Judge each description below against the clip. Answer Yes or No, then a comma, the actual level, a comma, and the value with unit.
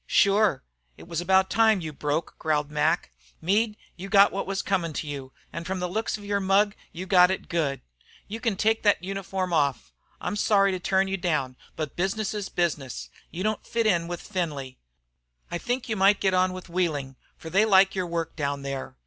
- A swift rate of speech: Yes, fast, 210 wpm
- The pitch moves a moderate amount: Yes, average, 3.7 semitones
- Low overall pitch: No, medium, 185 Hz